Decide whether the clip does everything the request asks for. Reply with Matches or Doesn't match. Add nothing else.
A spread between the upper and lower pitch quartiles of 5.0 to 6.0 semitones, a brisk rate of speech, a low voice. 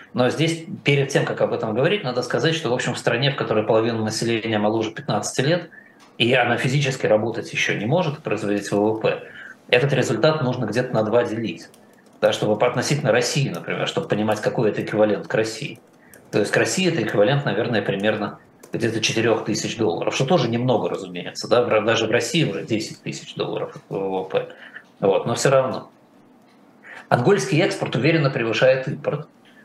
Matches